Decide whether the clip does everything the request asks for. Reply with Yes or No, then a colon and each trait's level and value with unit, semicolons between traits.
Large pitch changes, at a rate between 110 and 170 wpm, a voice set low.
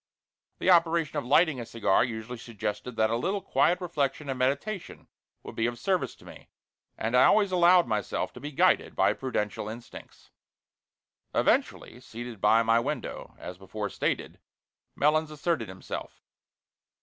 Yes: wide, 6.1 semitones; average, 150 wpm; low, 125 Hz